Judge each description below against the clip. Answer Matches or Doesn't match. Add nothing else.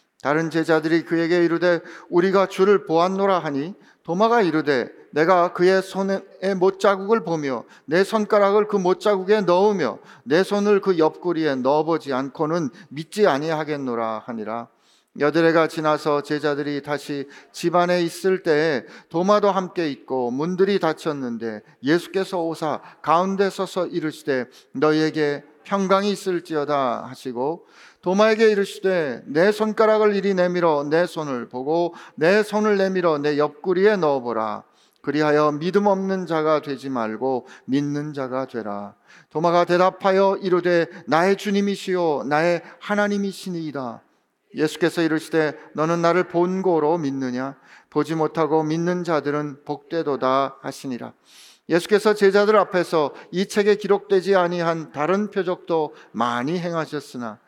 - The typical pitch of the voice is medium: Matches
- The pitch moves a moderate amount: Matches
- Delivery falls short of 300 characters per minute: Doesn't match